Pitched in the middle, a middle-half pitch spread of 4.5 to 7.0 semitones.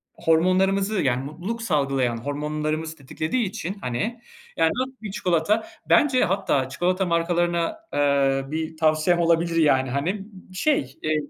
Yes: medium, 165 Hz; average, 4.8 semitones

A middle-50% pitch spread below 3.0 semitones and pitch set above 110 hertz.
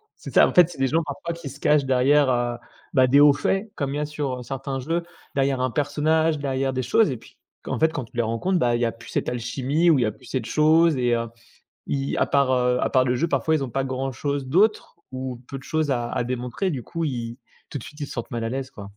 No: average, 3.3 semitones; low, 135 Hz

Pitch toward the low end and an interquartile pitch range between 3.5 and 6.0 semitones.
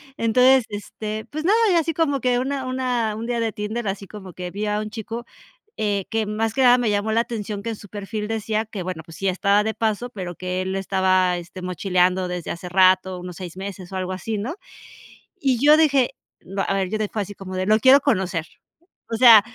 No: high, 210 Hz; average, 3.8 semitones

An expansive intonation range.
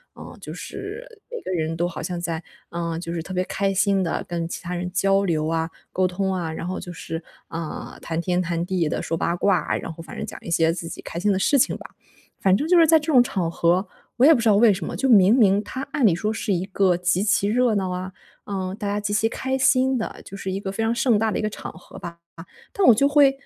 No: average, 4.3 semitones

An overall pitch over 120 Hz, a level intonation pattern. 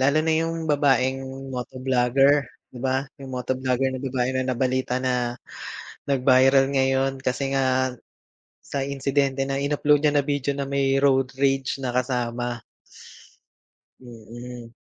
Yes: low, 135 Hz; narrow, 1.5 semitones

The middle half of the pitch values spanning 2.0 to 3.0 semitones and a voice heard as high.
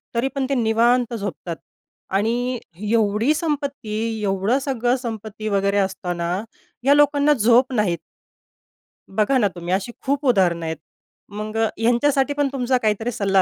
No: average, 4.4 semitones; high, 225 Hz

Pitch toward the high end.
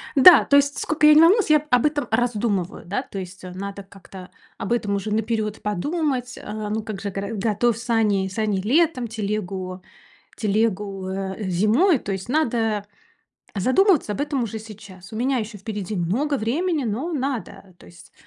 Yes: high, 215 Hz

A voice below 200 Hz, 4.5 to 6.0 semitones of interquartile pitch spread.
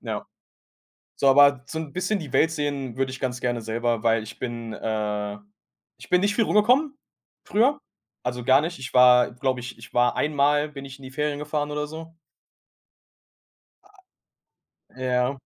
No: low, 135 Hz; average, 3.5 semitones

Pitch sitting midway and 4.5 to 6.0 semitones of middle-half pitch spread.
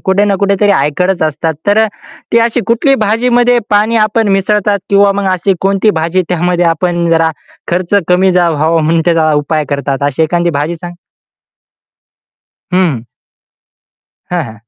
No: medium, 180 Hz; average, 3.8 semitones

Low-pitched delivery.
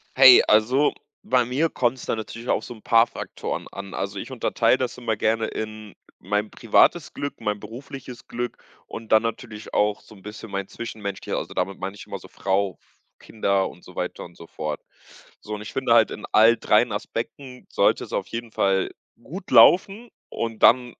Yes: low, 110 Hz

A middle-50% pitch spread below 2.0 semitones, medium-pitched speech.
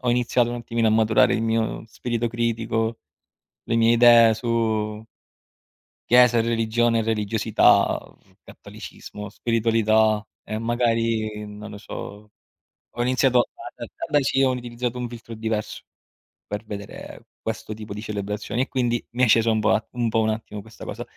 No: narrow, 1.5 semitones; low, 115 Hz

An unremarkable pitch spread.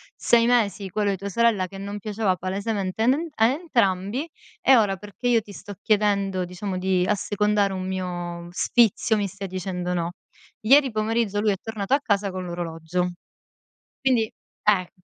Yes: average, 3.1 semitones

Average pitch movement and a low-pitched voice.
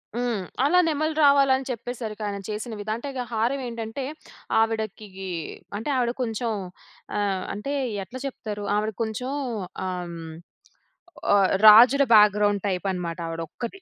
No: average, 3.5 semitones; high, 220 Hz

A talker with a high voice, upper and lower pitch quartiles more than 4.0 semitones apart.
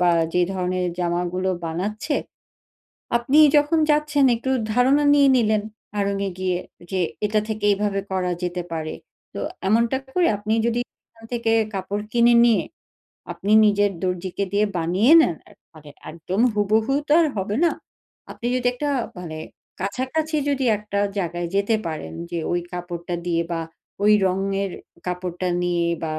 Yes: high, 200 Hz; average, 4.7 semitones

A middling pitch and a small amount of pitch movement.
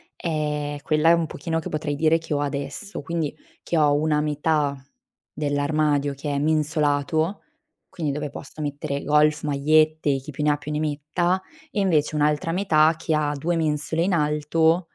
Yes: medium, 150 Hz; narrow, 1.6 semitones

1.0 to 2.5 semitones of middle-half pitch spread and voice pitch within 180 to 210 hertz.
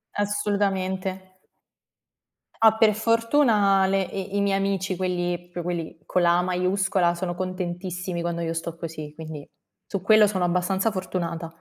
Yes: narrow, 2.2 semitones; medium, 185 Hz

